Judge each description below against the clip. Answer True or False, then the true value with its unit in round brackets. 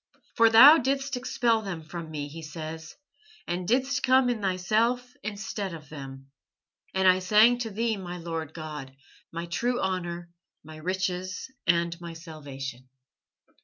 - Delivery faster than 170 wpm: False (145 wpm)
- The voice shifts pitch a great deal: True (6.0 semitones)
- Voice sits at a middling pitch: True (180 Hz)